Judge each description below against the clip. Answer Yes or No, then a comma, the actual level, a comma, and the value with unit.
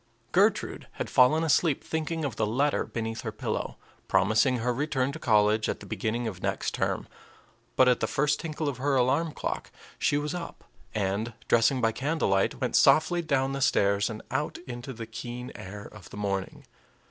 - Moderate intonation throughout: Yes, average, 4.9 semitones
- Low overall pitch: Yes, low, 125 Hz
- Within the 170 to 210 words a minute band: Yes, average, 180 wpm